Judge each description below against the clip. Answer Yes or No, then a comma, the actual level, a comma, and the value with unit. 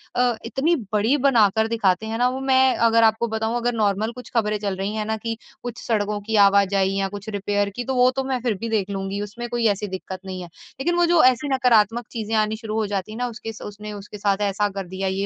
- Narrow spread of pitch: No, average, 3.0 semitones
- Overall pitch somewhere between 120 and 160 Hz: No, high, 215 Hz